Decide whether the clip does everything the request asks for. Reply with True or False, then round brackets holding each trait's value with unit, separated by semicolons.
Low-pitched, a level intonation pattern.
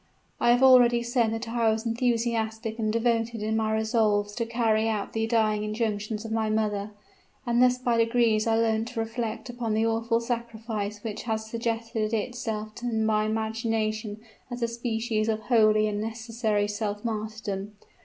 False (225 Hz; 1.4 semitones)